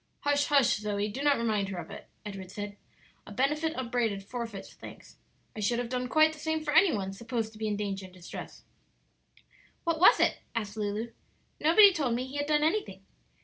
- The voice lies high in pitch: Yes, high, 235 Hz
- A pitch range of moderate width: No, wide, 6.0 semitones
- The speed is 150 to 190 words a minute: No, average, 200 wpm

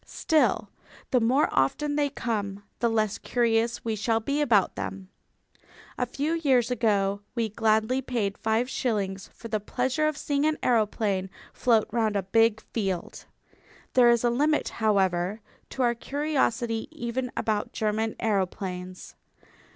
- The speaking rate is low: No, average, 145 wpm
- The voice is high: Yes, high, 225 Hz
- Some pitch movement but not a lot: Yes, average, 3.5 semitones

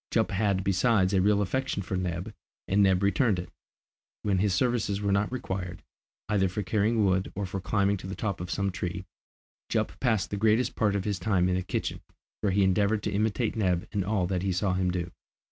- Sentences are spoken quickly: Yes, fast, 215 wpm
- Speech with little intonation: Yes, narrow, 2.2 semitones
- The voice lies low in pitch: Yes, low, 100 Hz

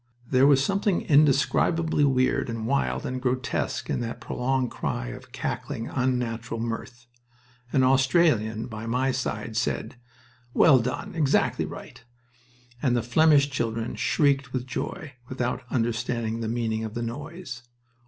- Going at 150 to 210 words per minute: No, slow, 135 wpm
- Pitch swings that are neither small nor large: Yes, average, 3.1 semitones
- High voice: No, low, 125 Hz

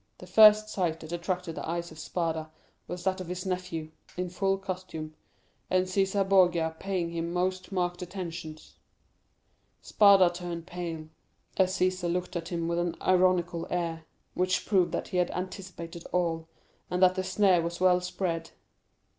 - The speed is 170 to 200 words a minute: No, average, 160 wpm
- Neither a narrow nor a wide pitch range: No, narrow, 1.6 semitones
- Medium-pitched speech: Yes, medium, 180 Hz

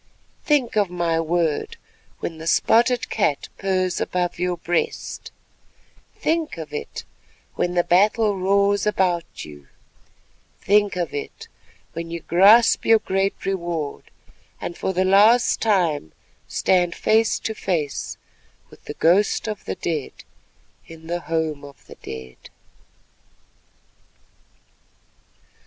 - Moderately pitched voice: Yes, medium, 180 Hz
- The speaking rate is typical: No, slow, 120 wpm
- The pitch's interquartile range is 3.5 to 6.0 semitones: Yes, average, 3.8 semitones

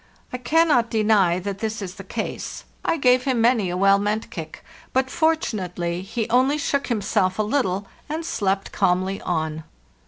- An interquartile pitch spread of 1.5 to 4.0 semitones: No, average, 5.2 semitones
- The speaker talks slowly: No, average, 165 wpm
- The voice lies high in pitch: Yes, high, 215 Hz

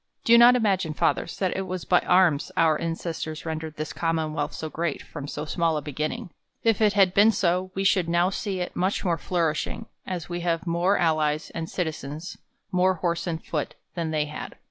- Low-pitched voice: No, medium, 170 Hz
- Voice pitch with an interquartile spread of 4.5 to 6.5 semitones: No, average, 2.8 semitones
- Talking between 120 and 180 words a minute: No, average, 200 wpm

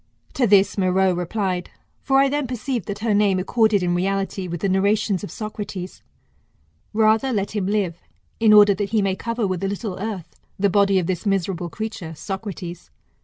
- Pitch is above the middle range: Yes, high, 200 Hz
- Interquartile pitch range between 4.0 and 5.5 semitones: No, narrow, 2.6 semitones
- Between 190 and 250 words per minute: No, average, 180 wpm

